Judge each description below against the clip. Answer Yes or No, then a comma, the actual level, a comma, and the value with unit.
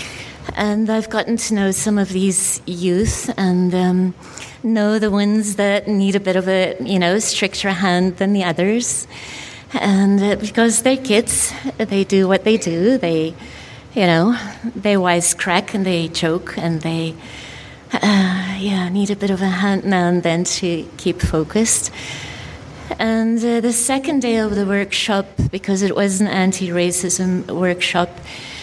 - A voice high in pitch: Yes, high, 195 Hz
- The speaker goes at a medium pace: Yes, average, 155 wpm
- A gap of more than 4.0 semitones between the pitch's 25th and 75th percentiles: No, average, 2.8 semitones